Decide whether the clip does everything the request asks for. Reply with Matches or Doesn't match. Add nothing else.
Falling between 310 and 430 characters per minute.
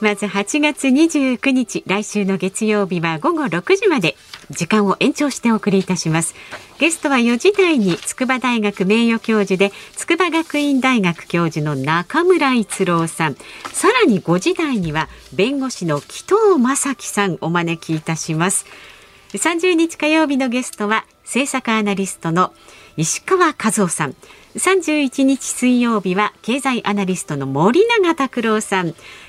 Doesn't match